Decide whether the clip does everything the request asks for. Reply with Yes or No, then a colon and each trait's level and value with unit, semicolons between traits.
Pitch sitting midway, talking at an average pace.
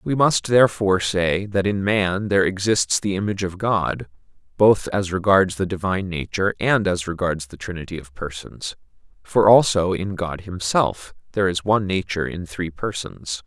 No: very low, 95 Hz; average, 170 wpm